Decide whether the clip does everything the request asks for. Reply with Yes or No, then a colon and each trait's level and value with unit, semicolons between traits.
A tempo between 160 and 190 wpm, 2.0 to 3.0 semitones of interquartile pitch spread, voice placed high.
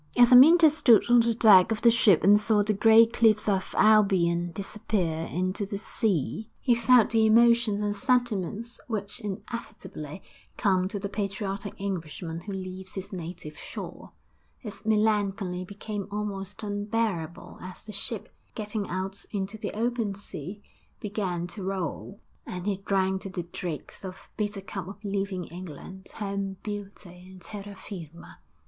No: average, 150 wpm; narrow, 2.6 semitones; high, 200 Hz